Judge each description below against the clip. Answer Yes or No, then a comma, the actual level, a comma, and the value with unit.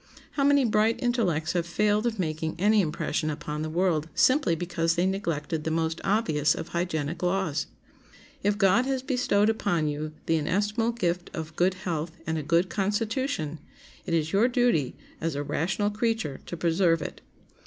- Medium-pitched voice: Yes, medium, 175 Hz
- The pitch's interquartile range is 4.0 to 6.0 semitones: Yes, average, 4.9 semitones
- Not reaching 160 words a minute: No, average, 170 wpm